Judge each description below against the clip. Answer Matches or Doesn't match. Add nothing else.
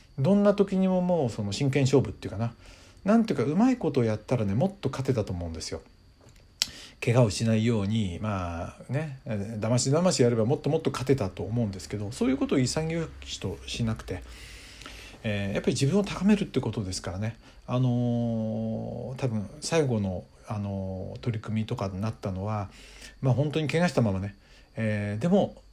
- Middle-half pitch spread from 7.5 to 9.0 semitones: Doesn't match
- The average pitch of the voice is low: Matches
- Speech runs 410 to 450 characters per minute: Doesn't match